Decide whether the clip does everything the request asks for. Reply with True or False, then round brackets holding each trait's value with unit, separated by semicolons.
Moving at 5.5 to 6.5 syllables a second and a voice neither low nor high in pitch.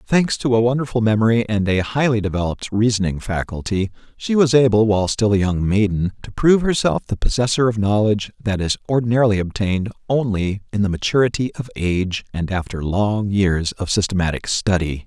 False (5.8 syllables/s; 105 Hz)